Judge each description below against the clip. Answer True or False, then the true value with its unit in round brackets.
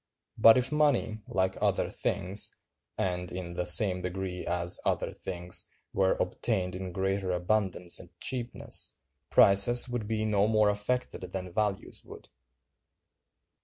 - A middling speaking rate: False (130 wpm)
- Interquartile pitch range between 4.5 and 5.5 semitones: False (3.1 semitones)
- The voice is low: True (95 Hz)